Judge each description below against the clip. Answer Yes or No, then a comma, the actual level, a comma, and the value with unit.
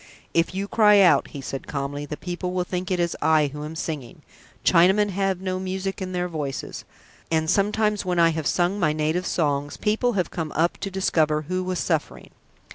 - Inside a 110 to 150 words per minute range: No, average, 200 wpm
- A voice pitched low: No, medium, 175 Hz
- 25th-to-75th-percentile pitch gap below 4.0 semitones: Yes, average, 3.5 semitones